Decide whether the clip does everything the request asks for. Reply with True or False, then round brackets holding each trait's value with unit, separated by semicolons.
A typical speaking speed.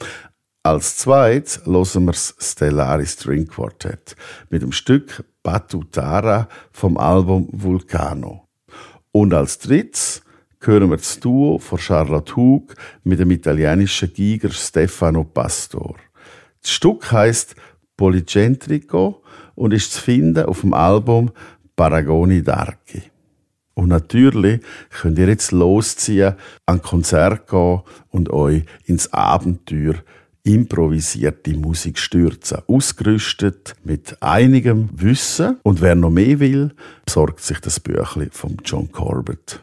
False (115 wpm)